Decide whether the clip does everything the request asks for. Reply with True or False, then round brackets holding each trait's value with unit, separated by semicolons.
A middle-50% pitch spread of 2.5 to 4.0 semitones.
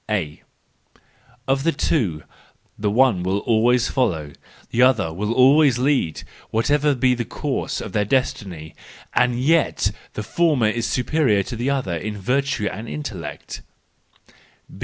False (4.8 semitones)